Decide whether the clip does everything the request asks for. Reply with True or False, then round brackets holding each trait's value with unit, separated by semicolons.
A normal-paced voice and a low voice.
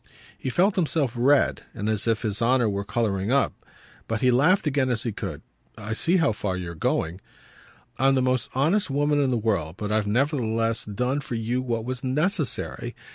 True (190 wpm; 120 Hz)